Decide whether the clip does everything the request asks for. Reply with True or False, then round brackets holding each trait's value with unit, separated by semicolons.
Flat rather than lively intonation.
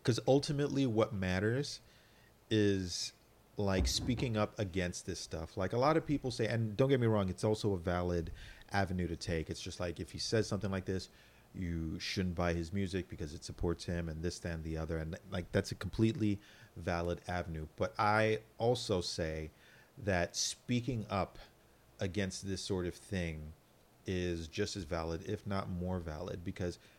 False (3.8 semitones)